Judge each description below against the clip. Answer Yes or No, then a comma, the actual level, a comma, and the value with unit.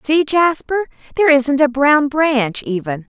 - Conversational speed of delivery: Yes, average, 150 wpm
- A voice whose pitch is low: No, very high, 280 Hz